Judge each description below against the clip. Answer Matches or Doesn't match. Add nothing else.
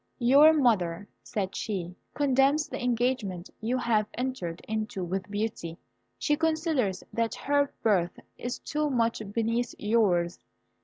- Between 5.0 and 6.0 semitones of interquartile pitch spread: Matches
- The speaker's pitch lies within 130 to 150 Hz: Doesn't match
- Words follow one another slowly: Matches